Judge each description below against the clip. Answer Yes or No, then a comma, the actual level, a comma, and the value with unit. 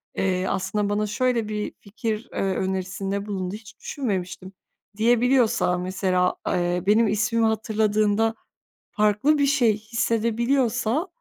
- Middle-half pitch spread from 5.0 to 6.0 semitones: No, average, 3.1 semitones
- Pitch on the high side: Yes, high, 215 Hz